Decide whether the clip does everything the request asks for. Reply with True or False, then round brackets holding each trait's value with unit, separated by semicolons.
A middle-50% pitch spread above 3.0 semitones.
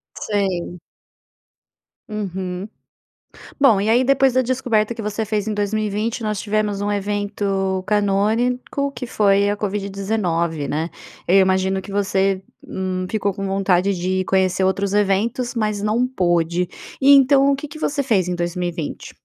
False (2.7 semitones)